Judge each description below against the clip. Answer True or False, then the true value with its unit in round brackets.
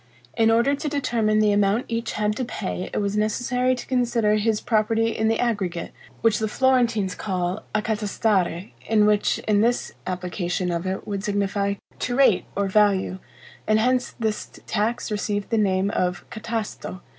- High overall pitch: True (215 Hz)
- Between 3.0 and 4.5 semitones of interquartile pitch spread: False (2.6 semitones)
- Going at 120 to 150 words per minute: False (165 wpm)